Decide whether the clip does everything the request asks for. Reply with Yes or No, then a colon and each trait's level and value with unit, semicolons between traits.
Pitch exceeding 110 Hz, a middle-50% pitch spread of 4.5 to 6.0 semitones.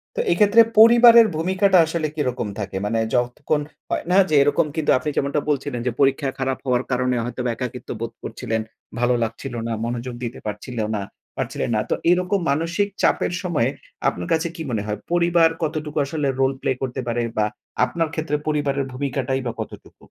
Yes: medium, 140 Hz; average, 5.0 semitones